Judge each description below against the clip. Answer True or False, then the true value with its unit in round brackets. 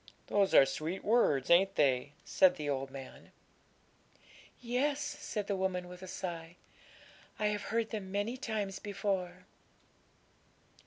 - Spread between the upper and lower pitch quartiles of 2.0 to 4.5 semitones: True (3.7 semitones)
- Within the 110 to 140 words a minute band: True (135 wpm)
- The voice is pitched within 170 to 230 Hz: True (190 Hz)